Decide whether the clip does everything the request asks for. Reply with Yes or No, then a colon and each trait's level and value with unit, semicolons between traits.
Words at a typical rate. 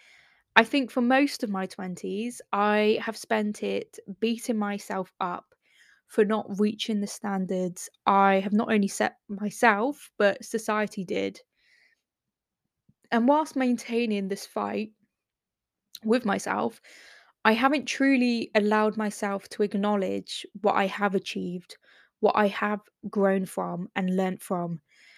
No: slow, 130 wpm